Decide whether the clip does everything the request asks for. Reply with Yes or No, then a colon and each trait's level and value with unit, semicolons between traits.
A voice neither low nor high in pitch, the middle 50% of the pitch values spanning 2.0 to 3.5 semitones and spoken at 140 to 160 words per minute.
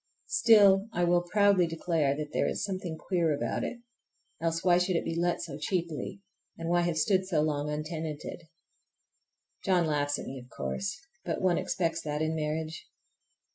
No: medium, 165 Hz; average, 3.2 semitones; average, 175 wpm